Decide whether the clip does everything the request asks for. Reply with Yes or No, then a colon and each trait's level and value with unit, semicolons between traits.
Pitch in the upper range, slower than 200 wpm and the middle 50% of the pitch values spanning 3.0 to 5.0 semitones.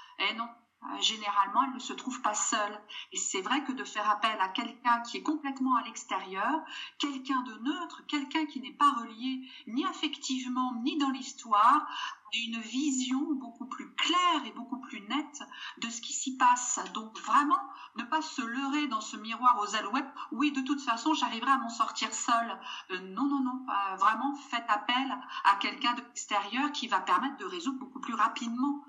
Yes: very high, 260 Hz; average, 190 wpm; average, 3.6 semitones